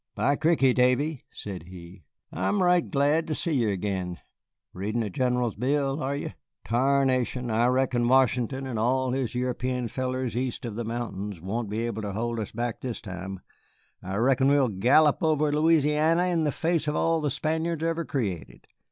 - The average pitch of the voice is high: No, low, 125 Hz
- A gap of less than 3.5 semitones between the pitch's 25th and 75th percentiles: No, average, 4.7 semitones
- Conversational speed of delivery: Yes, average, 175 wpm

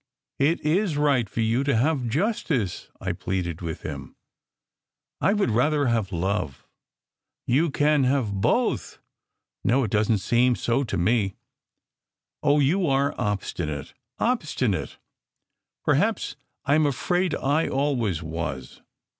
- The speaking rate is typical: No, slow, 130 wpm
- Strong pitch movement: Yes, wide, 7.0 semitones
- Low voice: Yes, low, 125 Hz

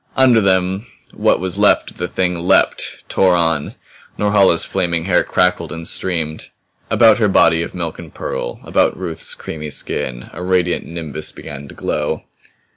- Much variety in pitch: No, narrow, 2.4 semitones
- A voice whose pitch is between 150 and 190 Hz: No, very low, 90 Hz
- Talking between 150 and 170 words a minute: Yes, average, 160 wpm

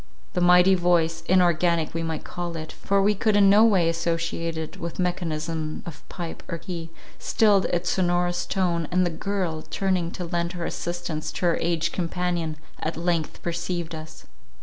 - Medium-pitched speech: Yes, medium, 175 Hz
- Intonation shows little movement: Yes, narrow, 1.5 semitones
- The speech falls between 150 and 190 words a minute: Yes, average, 170 wpm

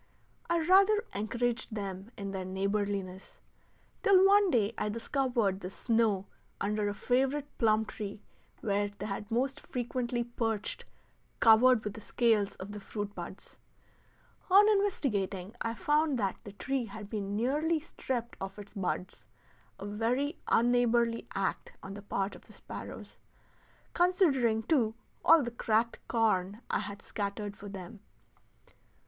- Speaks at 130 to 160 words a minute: Yes, average, 140 wpm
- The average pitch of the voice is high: Yes, high, 220 Hz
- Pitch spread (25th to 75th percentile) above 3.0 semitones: Yes, average, 4.0 semitones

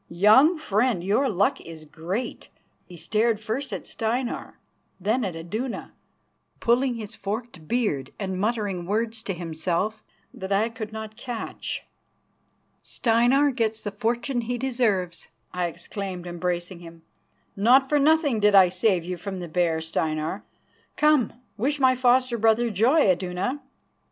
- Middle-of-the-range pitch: No, high, 215 Hz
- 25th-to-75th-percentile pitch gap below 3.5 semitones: No, average, 5.1 semitones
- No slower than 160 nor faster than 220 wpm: No, average, 140 wpm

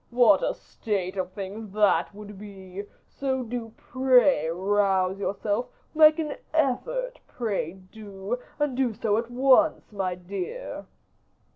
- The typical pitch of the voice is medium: No, high, 210 Hz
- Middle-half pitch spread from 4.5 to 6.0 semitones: Yes, average, 4.9 semitones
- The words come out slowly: Yes, slow, 130 wpm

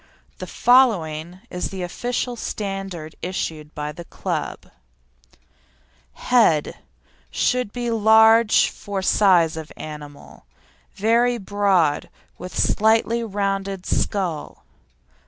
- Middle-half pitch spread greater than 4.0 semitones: Yes, average, 5.2 semitones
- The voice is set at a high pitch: Yes, high, 195 Hz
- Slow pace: Yes, slow, 100 wpm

